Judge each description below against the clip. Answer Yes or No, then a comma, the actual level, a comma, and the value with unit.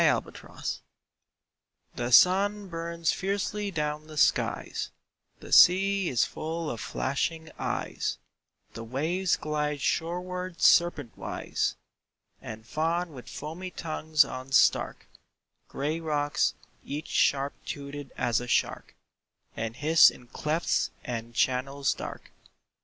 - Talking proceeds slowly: Yes, slow, 115 wpm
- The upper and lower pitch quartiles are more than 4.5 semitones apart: No, average, 4.1 semitones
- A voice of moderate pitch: Yes, medium, 155 Hz